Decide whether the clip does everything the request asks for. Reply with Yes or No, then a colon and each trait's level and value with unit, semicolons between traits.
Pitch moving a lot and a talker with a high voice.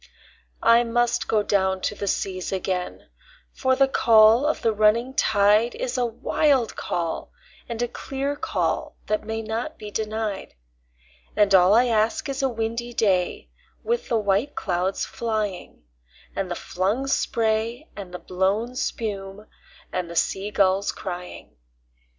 No: average, 3.6 semitones; high, 215 Hz